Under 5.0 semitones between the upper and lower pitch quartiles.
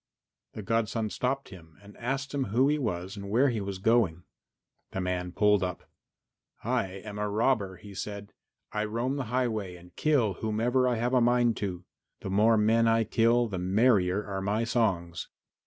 Yes: average, 3.8 semitones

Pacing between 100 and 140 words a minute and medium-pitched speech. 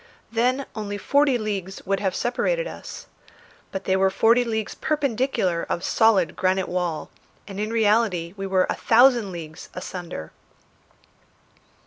No: slow, 135 wpm; high, 205 Hz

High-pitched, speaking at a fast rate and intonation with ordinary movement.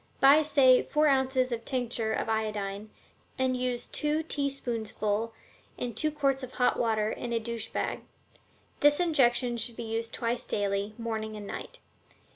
No: high, 240 Hz; average, 160 wpm; average, 3.5 semitones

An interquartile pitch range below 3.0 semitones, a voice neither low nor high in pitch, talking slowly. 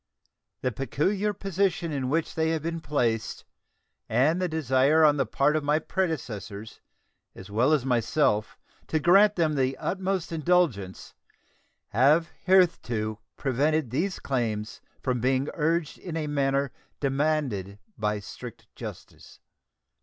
No: average, 5.0 semitones; medium, 145 Hz; slow, 130 wpm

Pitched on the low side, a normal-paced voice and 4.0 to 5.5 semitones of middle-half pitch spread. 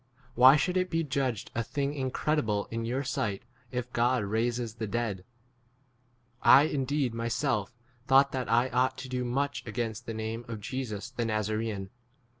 No: low, 120 Hz; average, 170 wpm; average, 3.1 semitones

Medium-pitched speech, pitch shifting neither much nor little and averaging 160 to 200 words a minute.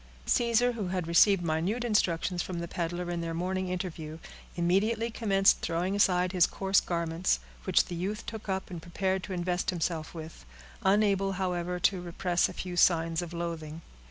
No: medium, 180 Hz; narrow, 2.3 semitones; average, 170 wpm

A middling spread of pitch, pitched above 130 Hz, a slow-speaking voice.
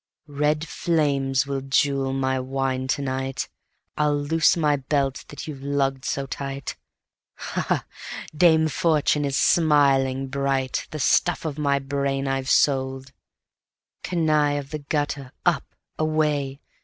No: narrow, 1.9 semitones; medium, 140 Hz; slow, 130 wpm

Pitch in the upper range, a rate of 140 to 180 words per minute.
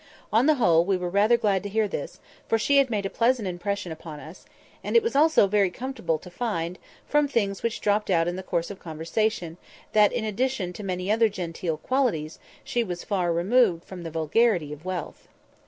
No: high, 195 Hz; fast, 205 wpm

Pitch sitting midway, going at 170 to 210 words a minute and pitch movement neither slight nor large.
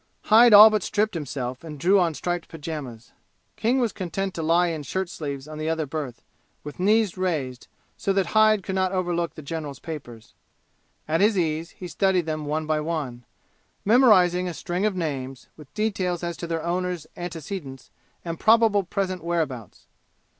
Yes: medium, 170 Hz; average, 175 wpm; average, 3.9 semitones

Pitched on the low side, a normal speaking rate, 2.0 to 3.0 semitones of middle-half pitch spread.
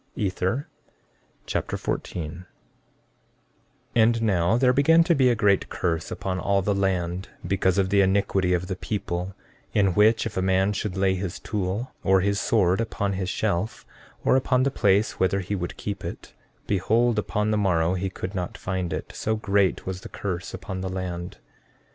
Yes: very low, 95 Hz; average, 180 wpm; narrow, 2.4 semitones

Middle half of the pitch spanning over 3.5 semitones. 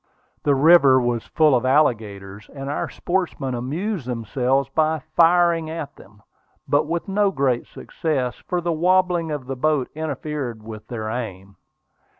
Yes: average, 5.1 semitones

